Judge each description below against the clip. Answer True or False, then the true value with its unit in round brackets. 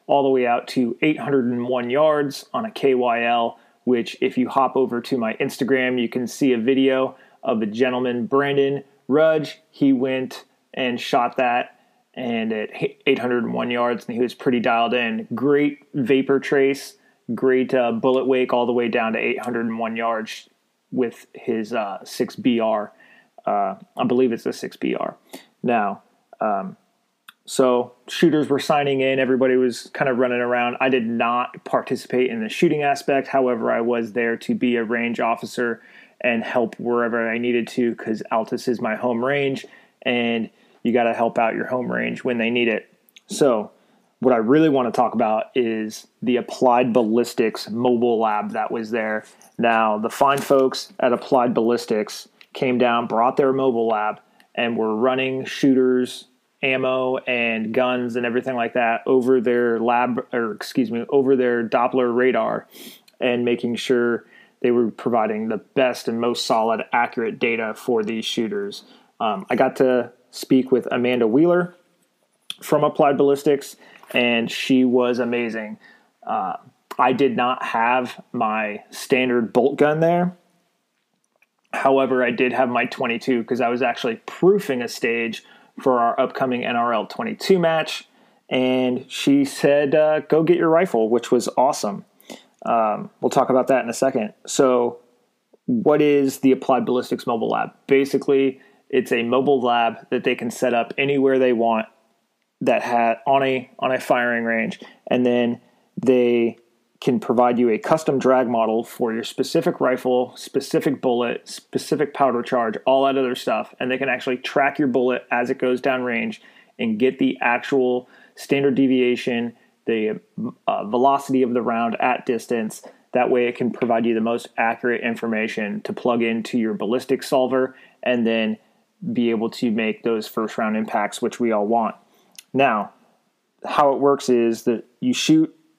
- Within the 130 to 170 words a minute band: True (165 wpm)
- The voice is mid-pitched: False (125 Hz)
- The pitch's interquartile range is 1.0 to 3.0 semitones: True (2.4 semitones)